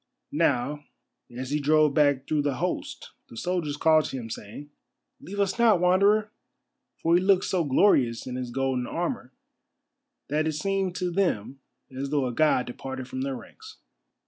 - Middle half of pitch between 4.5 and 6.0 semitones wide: Yes, wide, 5.6 semitones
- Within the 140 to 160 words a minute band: No, average, 170 wpm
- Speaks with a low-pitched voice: No, medium, 150 Hz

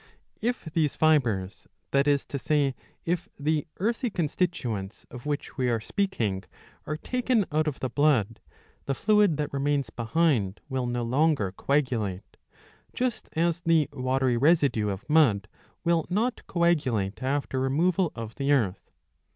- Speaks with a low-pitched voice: No, medium, 145 Hz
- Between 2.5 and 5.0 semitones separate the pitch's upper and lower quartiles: No, wide, 5.6 semitones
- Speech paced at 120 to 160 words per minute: Yes, average, 150 wpm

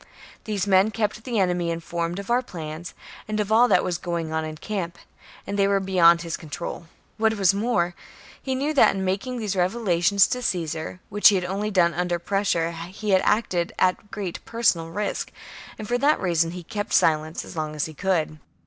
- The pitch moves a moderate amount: Yes, average, 3.8 semitones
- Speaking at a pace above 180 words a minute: Yes, fast, 205 wpm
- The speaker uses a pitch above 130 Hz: Yes, medium, 185 Hz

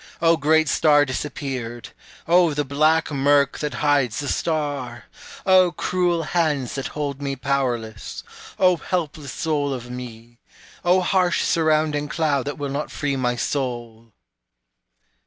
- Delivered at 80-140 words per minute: Yes, slow, 135 wpm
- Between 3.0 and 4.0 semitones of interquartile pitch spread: Yes, average, 3.4 semitones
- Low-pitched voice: No, medium, 145 Hz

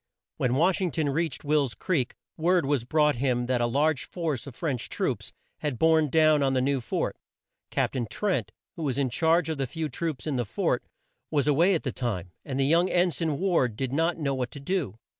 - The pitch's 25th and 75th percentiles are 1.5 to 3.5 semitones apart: No, average, 3.9 semitones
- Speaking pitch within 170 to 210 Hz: No, medium, 145 Hz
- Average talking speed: No, fast, 225 wpm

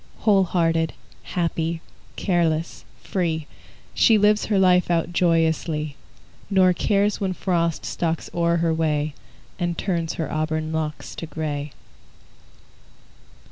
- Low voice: No, medium, 165 Hz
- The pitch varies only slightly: Yes, narrow, 2.3 semitones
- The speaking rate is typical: No, slow, 115 wpm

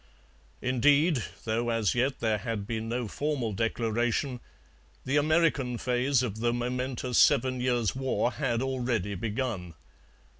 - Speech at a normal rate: No, slow, 125 wpm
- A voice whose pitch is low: Yes, low, 120 Hz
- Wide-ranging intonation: No, narrow, 2.4 semitones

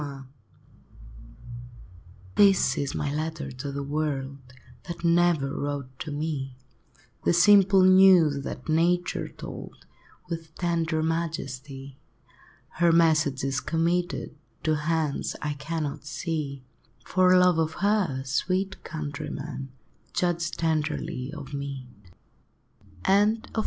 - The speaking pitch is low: No, medium, 155 Hz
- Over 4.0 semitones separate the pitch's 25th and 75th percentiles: No, average, 3.5 semitones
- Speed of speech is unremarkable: No, slow, 110 wpm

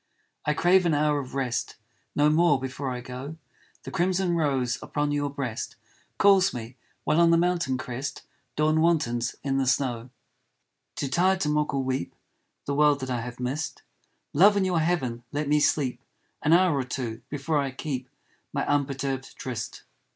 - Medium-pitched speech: Yes, medium, 145 Hz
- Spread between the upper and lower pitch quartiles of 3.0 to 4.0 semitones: Yes, average, 3.6 semitones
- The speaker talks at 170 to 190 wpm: Yes, average, 175 wpm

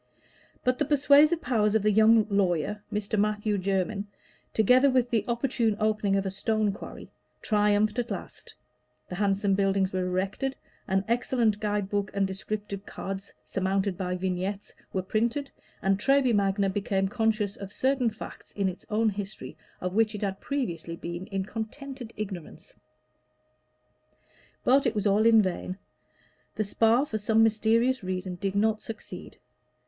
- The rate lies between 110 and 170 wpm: Yes, average, 155 wpm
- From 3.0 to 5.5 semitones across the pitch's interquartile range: No, narrow, 2.6 semitones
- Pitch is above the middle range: Yes, high, 210 Hz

